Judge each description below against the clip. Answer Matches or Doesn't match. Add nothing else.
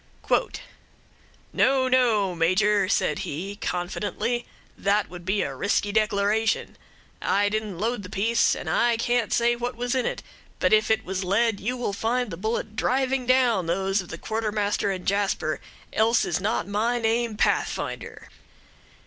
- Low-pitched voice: Doesn't match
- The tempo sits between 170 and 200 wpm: Doesn't match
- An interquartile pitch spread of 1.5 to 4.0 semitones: Matches